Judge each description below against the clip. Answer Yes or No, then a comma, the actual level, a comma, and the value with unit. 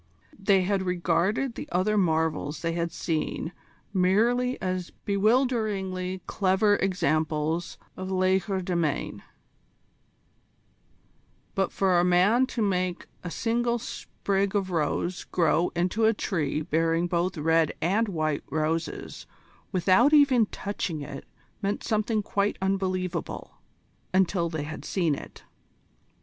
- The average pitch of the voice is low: No, medium, 185 Hz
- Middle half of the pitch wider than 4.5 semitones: No, average, 3.3 semitones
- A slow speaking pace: Yes, slow, 115 wpm